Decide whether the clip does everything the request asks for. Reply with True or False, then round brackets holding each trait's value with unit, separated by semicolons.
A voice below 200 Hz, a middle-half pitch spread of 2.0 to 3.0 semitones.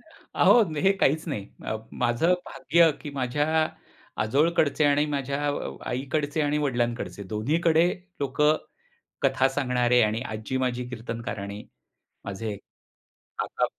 False (135 Hz; 3.8 semitones)